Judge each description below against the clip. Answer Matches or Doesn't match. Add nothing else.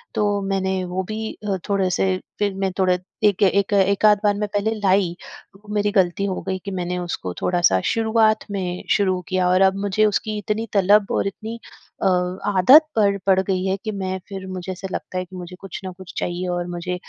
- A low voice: Doesn't match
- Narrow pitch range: Matches